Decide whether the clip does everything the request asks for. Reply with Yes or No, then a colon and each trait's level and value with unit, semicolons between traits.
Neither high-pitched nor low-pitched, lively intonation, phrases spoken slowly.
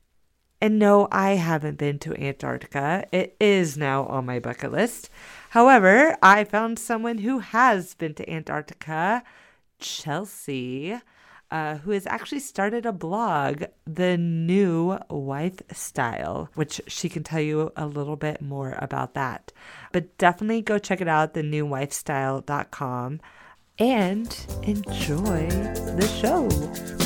Yes: medium, 170 Hz; wide, 5.9 semitones; slow, 125 wpm